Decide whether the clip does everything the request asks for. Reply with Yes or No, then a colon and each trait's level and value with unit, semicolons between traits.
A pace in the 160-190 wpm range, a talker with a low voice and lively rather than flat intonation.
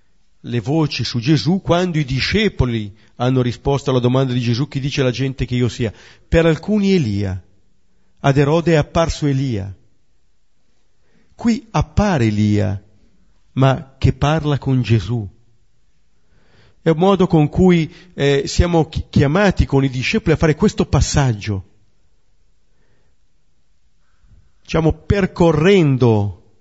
No: average, 120 wpm; low, 130 Hz; wide, 7.1 semitones